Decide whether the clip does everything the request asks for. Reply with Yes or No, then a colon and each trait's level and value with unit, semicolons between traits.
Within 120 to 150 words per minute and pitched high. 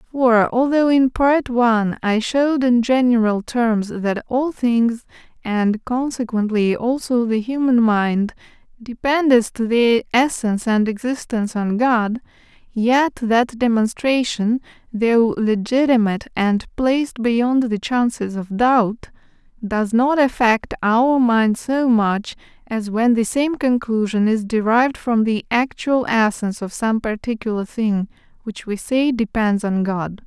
Yes: slow, 135 wpm; high, 235 Hz